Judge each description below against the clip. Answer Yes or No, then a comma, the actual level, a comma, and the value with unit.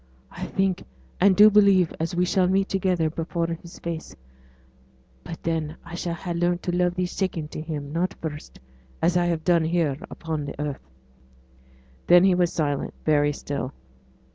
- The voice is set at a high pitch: No, medium, 170 Hz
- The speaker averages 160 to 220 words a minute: Yes, average, 170 wpm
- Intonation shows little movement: Yes, narrow, 2.3 semitones